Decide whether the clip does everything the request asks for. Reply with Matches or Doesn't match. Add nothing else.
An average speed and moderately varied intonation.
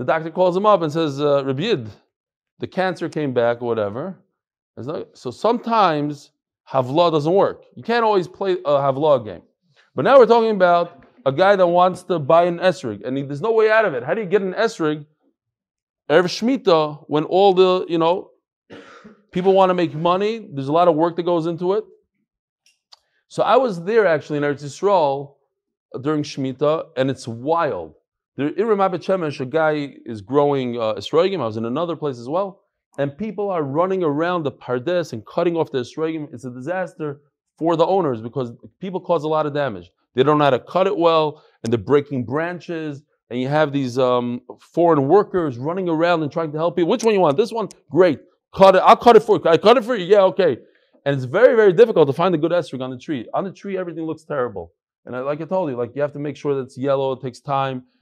Doesn't match